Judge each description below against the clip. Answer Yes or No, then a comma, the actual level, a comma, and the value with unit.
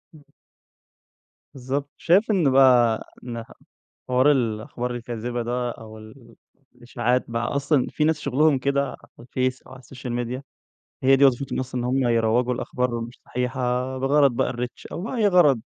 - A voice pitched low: Yes, low, 125 Hz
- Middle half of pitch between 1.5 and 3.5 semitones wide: Yes, narrow, 2.5 semitones